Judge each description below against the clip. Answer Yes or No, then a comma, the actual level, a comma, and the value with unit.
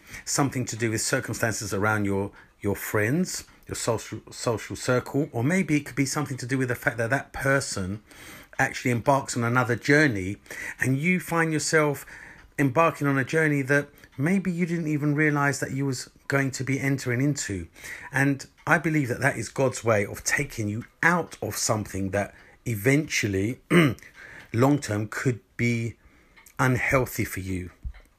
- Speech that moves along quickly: No, average, 165 wpm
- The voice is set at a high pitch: No, low, 135 Hz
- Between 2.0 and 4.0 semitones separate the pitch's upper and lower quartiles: No, average, 4.6 semitones